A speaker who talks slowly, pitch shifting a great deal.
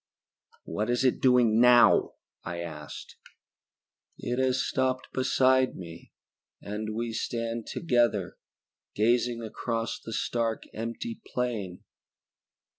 No: slow, 105 wpm; narrow, 2.5 semitones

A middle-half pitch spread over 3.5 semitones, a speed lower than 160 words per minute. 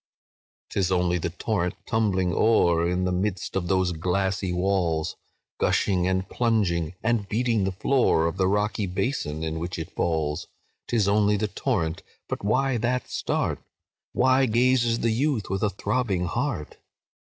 Yes: average, 4.1 semitones; average, 150 wpm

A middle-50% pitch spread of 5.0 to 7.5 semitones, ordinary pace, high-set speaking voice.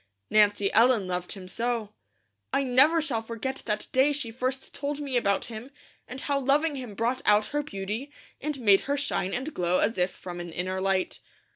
Yes: wide, 5.6 semitones; average, 190 wpm; high, 235 Hz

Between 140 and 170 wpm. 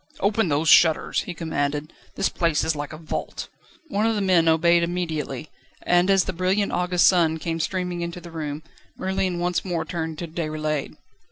No: average, 180 wpm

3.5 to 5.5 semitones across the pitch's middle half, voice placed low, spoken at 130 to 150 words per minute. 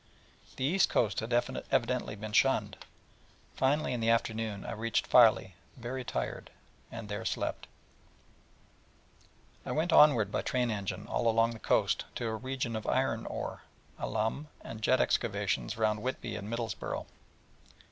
No: average, 2.8 semitones; low, 115 Hz; average, 145 wpm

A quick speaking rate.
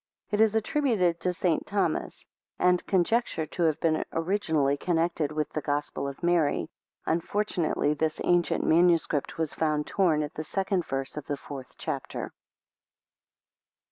No: average, 140 wpm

